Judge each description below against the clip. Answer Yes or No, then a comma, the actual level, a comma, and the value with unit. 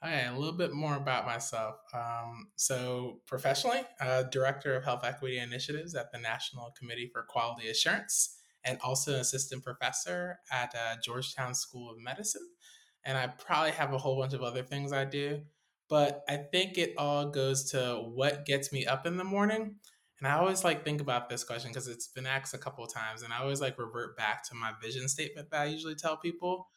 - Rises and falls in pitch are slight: No, average, 3.6 semitones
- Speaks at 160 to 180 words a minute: No, fast, 205 wpm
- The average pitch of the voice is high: No, low, 135 Hz